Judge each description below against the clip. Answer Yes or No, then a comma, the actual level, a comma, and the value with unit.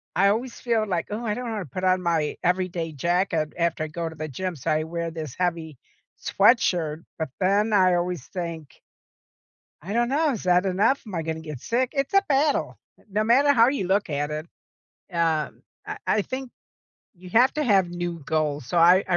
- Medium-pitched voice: Yes, medium, 180 Hz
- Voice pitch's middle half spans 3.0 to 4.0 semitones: No, average, 5.0 semitones